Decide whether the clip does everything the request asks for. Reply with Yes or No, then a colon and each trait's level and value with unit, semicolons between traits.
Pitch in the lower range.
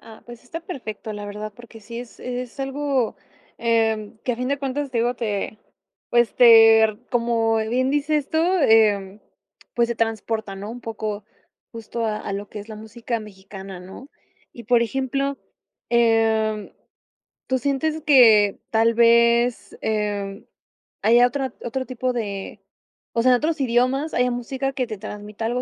No: high, 230 Hz